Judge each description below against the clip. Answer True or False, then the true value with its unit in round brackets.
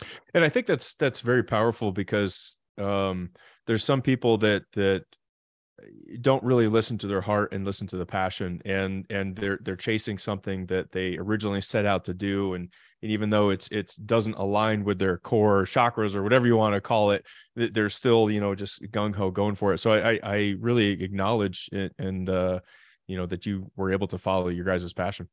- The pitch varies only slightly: True (2.3 semitones)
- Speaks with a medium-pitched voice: False (100 Hz)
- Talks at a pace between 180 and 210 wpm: True (205 wpm)